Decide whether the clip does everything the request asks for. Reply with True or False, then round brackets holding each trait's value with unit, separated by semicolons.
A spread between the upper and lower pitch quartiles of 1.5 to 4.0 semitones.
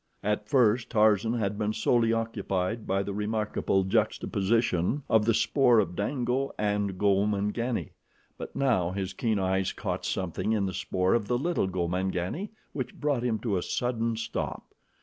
True (3.4 semitones)